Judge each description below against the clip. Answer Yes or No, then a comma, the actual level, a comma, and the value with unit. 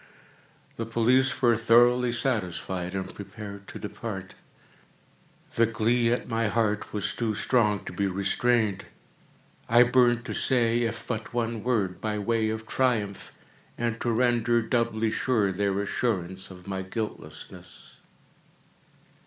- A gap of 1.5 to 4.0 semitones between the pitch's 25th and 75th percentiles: Yes, average, 2.9 semitones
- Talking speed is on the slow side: Yes, slow, 130 wpm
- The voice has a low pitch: Yes, low, 115 Hz